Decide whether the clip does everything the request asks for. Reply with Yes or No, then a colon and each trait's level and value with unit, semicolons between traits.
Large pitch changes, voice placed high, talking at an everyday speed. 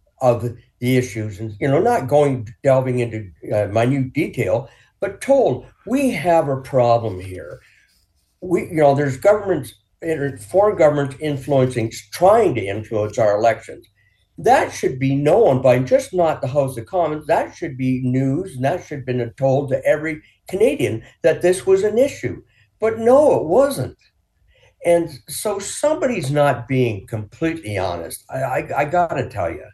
No: wide, 5.8 semitones; low, 135 Hz; average, 160 wpm